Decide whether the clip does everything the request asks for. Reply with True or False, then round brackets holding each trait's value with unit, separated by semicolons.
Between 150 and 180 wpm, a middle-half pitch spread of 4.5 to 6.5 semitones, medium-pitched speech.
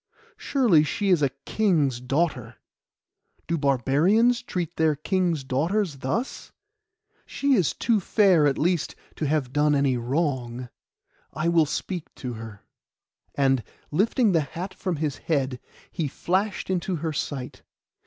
False (135 wpm; 5.3 semitones; 155 Hz)